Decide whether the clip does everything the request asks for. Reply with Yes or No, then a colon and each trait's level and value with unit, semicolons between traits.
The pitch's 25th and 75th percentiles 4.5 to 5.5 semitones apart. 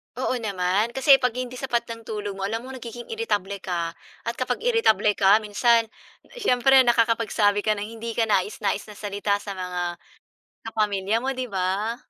No: average, 3.2 semitones